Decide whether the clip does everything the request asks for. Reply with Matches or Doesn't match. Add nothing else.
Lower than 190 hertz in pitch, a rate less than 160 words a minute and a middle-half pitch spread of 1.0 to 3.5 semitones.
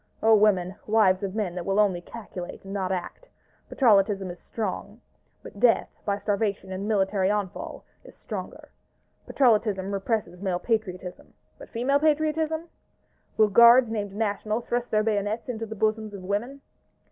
Doesn't match